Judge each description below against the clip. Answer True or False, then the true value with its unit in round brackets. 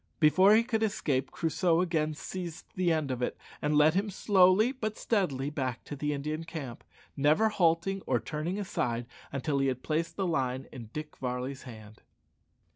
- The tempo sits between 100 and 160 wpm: False (175 wpm)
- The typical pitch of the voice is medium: True (155 Hz)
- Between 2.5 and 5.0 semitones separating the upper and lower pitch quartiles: False (5.5 semitones)